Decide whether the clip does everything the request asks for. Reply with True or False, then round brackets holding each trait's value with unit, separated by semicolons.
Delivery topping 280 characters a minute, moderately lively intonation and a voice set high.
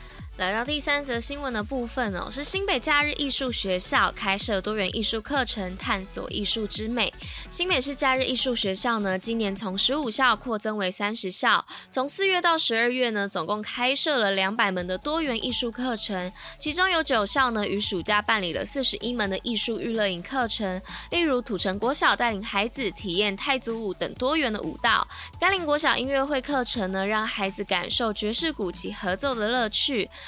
True (295 characters per minute; 5.0 semitones; 230 Hz)